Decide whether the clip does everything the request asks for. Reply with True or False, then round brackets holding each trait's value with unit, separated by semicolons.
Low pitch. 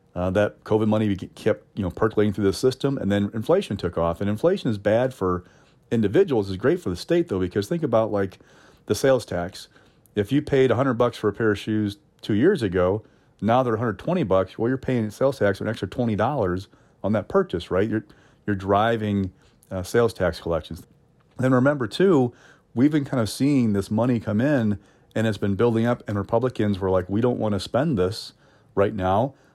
True (110 Hz)